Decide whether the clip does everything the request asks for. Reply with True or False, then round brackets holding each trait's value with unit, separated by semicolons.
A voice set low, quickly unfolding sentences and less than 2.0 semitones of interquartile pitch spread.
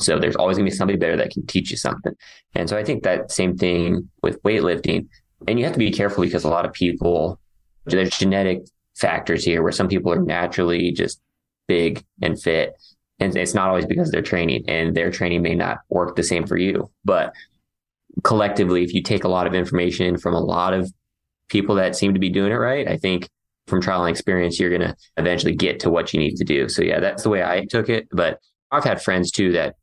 True (90 Hz; 230 wpm; 1.4 semitones)